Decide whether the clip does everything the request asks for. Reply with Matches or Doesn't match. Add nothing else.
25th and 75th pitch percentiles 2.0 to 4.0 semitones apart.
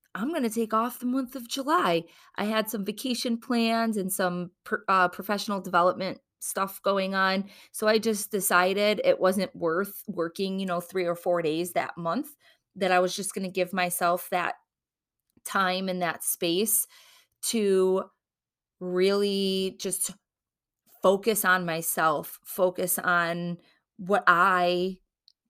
Matches